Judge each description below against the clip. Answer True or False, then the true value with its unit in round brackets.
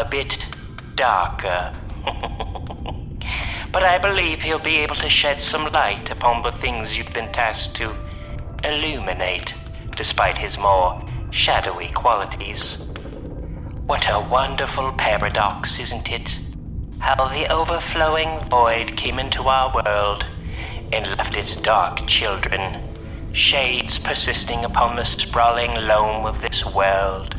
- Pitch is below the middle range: True (110 Hz)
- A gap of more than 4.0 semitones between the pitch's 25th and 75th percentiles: True (5.3 semitones)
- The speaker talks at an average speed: False (120 wpm)